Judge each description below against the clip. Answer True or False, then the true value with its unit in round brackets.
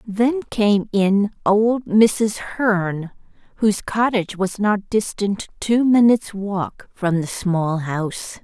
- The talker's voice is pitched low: False (205 Hz)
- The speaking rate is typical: False (130 wpm)